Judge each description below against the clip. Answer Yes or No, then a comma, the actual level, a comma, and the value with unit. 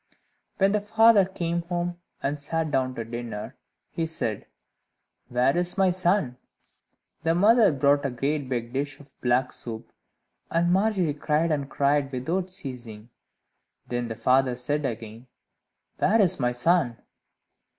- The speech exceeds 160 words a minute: No, average, 140 wpm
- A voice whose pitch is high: No, medium, 145 Hz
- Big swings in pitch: Yes, wide, 5.9 semitones